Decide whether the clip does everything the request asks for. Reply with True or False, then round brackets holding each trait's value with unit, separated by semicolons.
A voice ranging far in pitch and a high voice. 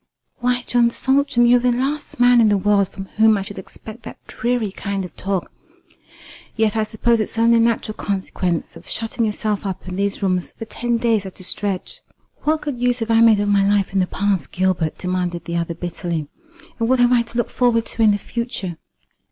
False (3.7 semitones; 215 Hz)